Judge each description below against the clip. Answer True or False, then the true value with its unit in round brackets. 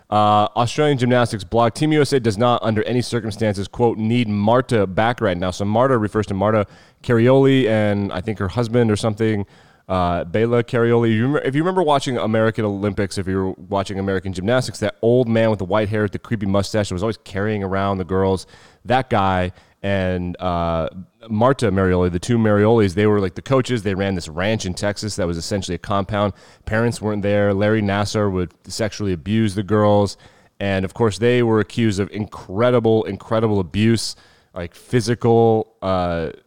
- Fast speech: False (180 wpm)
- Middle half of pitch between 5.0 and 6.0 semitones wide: False (3.2 semitones)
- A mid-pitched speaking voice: False (105 Hz)